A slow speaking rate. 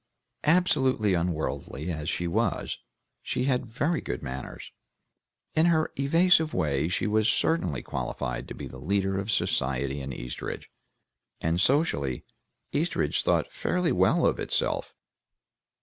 Yes: slow, 130 wpm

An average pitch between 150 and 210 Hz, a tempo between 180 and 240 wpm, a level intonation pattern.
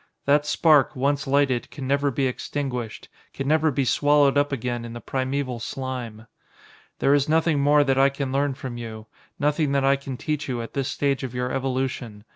No: low, 135 Hz; average, 195 wpm; narrow, 2.2 semitones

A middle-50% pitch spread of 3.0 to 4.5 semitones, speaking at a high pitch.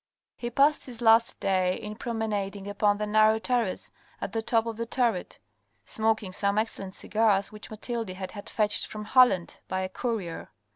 No: narrow, 2.5 semitones; high, 215 Hz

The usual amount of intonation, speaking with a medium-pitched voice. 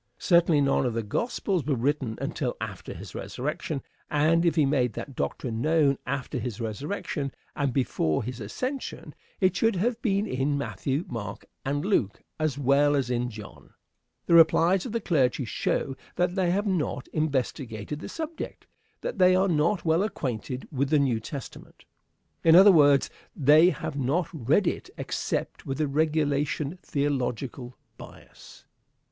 Yes: average, 4.9 semitones; medium, 145 Hz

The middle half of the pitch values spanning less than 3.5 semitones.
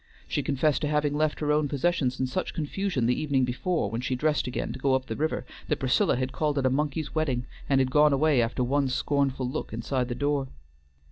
Yes: narrow, 2.6 semitones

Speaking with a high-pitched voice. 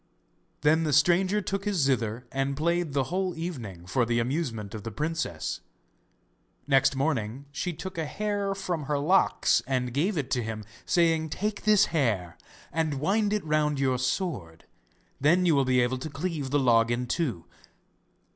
No: medium, 145 Hz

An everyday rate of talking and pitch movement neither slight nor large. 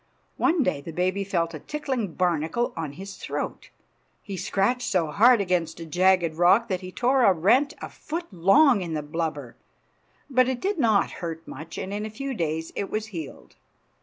No: average, 190 wpm; wide, 6.4 semitones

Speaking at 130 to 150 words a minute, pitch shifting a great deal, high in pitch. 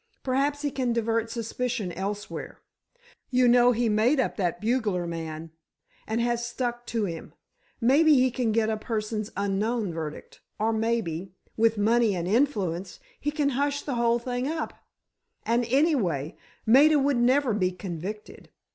No: slow, 135 wpm; average, 3.9 semitones; high, 230 Hz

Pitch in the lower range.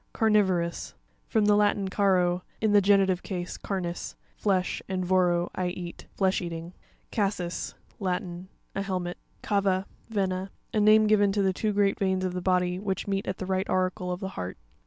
No: high, 190 Hz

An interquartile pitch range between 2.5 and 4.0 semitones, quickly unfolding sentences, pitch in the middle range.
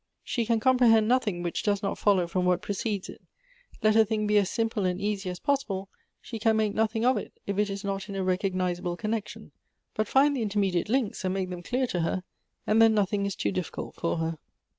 No: average, 3.2 semitones; fast, 225 wpm; high, 205 Hz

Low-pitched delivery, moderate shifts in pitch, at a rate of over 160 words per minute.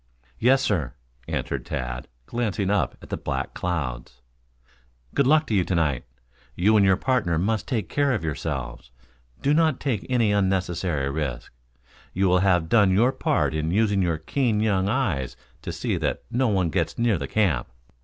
No: very low, 95 Hz; wide, 5.9 semitones; average, 175 wpm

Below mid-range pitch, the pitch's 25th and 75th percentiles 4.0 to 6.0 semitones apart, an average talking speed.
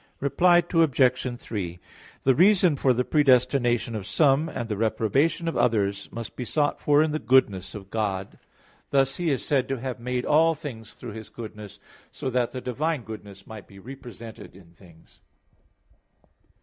Yes: low, 125 Hz; average, 4.8 semitones; average, 160 wpm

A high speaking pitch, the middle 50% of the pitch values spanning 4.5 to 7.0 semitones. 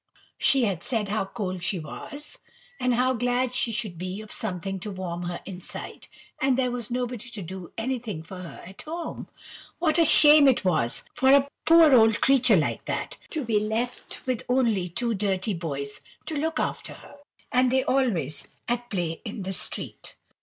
Yes: high, 225 Hz; wide, 5.6 semitones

